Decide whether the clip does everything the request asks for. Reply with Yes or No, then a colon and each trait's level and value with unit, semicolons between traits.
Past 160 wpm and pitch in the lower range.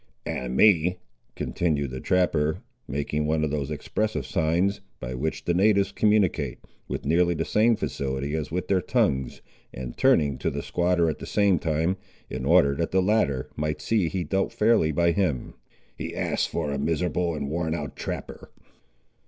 Yes: average, 170 wpm; very low, 80 Hz